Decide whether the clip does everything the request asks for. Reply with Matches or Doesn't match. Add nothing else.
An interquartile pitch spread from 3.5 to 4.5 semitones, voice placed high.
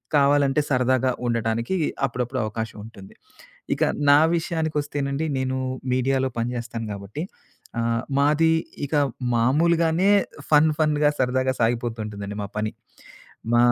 Doesn't match